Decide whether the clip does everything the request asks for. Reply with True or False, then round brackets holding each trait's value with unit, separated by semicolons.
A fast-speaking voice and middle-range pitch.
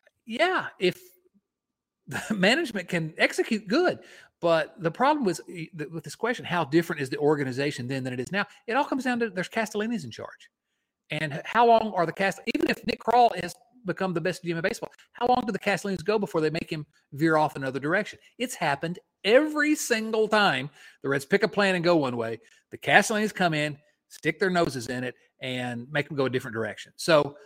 True (210 wpm; 180 Hz)